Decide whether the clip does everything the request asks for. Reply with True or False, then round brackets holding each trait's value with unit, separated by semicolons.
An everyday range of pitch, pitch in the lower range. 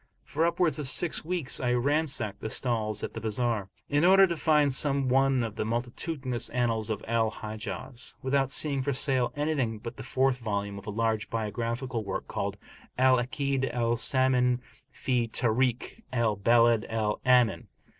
True (3.3 semitones; 125 Hz)